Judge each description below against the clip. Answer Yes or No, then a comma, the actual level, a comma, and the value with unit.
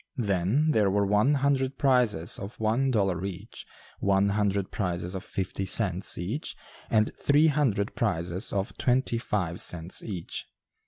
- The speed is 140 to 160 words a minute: Yes, average, 145 wpm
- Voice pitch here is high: No, low, 100 Hz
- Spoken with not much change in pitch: No, average, 4.8 semitones